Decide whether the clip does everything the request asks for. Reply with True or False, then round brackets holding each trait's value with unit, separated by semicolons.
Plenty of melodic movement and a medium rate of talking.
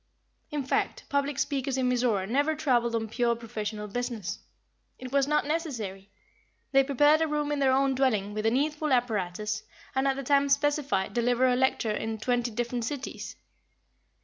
False (4.0 semitones; 170 wpm)